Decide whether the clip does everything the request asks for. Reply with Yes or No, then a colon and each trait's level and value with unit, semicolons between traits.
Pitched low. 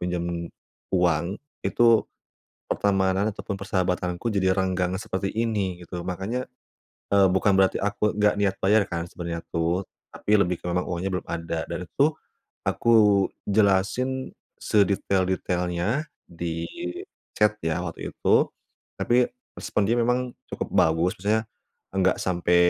Yes: very low, 95 Hz